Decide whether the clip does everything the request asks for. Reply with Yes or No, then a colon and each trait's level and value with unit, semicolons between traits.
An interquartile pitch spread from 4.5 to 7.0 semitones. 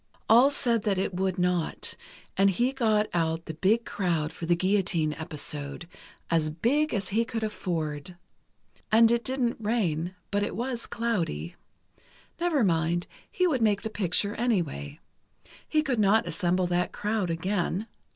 Yes: average, 5.3 semitones